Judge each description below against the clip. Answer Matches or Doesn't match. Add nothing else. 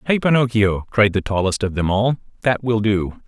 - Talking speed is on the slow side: Doesn't match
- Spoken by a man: Matches